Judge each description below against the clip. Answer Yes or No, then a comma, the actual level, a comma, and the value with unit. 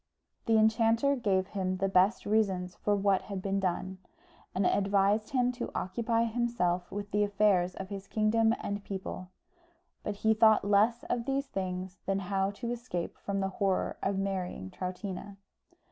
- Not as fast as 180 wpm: Yes, average, 160 wpm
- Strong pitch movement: No, narrow, 2.6 semitones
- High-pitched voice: Yes, high, 200 Hz